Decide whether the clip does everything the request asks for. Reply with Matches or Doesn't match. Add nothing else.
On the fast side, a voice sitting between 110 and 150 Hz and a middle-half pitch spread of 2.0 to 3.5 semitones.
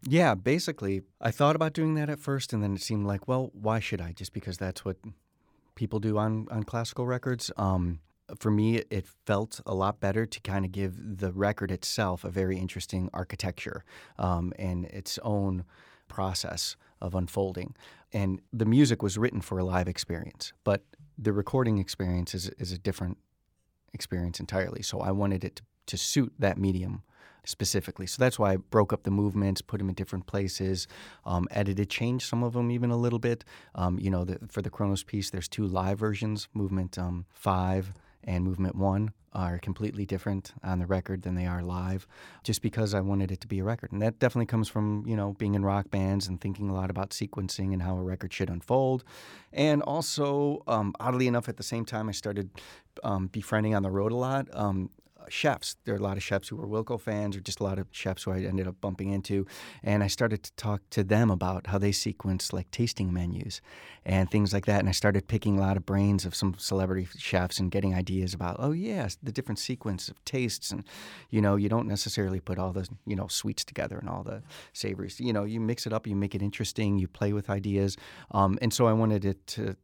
Doesn't match